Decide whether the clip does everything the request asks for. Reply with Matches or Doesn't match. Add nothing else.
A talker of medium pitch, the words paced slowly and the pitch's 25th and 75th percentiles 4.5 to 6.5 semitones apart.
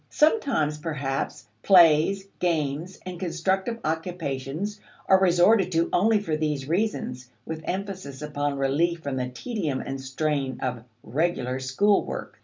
Matches